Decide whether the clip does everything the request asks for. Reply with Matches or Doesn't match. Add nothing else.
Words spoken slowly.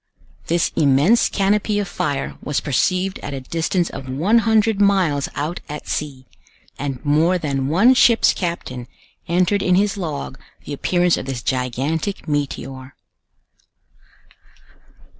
Matches